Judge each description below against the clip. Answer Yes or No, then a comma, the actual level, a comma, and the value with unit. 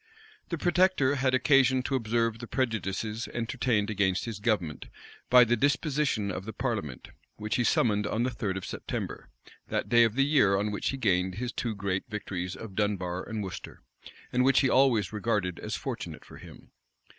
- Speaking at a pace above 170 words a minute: Yes, average, 180 wpm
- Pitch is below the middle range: Yes, low, 110 Hz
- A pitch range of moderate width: Yes, average, 4.4 semitones